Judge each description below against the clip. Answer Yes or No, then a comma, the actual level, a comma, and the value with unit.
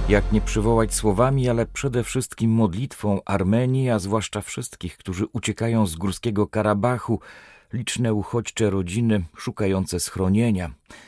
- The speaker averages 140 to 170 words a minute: No, average, 120 wpm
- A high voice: No, low, 110 Hz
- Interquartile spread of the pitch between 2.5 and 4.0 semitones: Yes, average, 2.9 semitones